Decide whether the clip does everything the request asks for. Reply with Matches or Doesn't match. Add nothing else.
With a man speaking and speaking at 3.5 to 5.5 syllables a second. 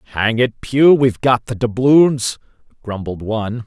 Matches